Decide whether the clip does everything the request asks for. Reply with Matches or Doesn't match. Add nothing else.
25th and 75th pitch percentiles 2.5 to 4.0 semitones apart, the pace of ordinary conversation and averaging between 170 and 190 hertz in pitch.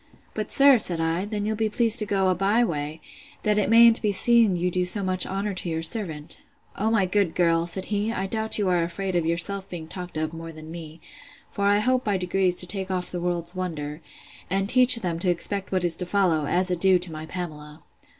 Doesn't match